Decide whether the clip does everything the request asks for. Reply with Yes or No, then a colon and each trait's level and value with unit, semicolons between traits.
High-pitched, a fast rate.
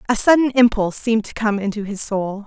Yes: high, 220 Hz; fast, 220 wpm